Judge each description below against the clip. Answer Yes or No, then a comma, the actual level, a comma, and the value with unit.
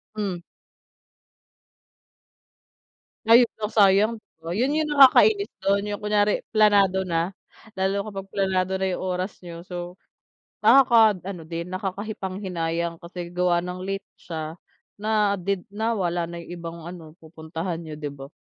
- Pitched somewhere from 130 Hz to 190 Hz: Yes, medium, 185 Hz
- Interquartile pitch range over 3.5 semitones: No, average, 3.2 semitones